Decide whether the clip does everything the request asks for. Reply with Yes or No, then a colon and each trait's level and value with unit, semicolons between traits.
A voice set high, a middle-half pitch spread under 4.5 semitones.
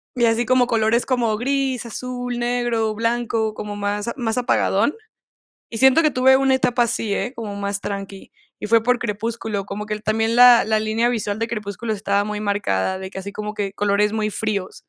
Yes: high, 220 Hz; average, 2.8 semitones